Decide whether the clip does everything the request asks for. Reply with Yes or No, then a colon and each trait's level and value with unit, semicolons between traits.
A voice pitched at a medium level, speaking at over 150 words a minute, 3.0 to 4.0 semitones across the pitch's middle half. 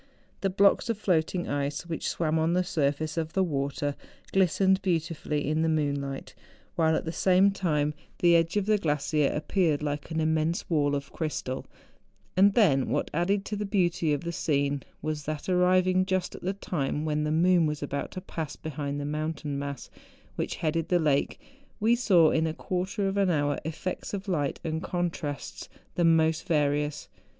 Yes: medium, 160 Hz; average, 180 wpm; average, 3.7 semitones